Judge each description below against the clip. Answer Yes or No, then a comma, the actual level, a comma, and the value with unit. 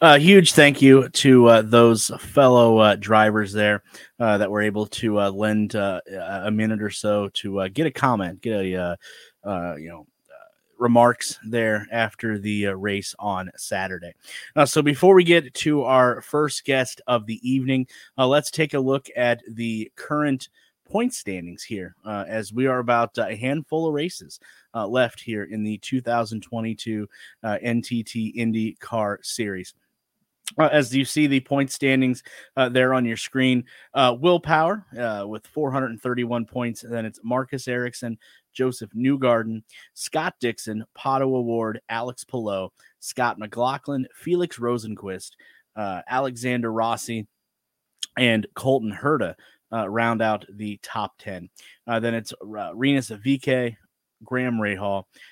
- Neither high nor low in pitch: No, low, 120 Hz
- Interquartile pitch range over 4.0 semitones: No, average, 3.7 semitones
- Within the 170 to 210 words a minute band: No, average, 155 wpm